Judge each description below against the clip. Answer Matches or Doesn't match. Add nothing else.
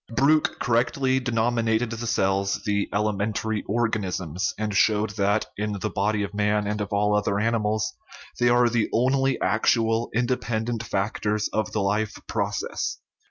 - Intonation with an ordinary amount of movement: Doesn't match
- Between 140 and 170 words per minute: Matches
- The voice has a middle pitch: Doesn't match